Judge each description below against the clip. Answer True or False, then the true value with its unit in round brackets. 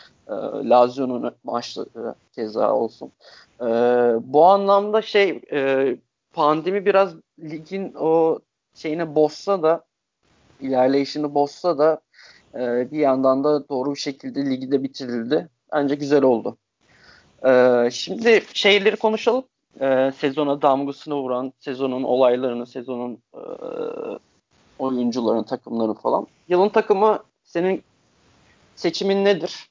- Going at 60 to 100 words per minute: True (95 wpm)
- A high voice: False (145 Hz)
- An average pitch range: False (6.1 semitones)